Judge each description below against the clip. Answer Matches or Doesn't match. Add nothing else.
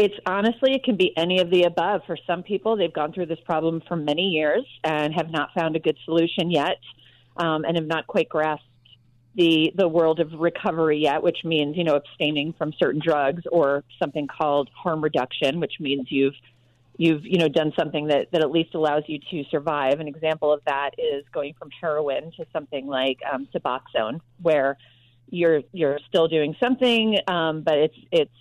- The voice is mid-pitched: Matches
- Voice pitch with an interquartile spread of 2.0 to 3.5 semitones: Matches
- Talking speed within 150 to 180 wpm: Doesn't match